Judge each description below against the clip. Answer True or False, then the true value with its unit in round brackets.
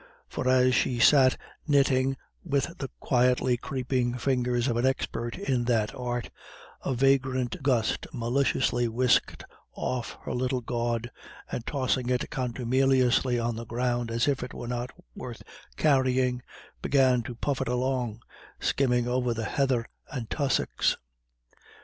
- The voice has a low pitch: True (125 Hz)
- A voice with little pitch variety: True (1.7 semitones)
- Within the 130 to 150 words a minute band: True (135 wpm)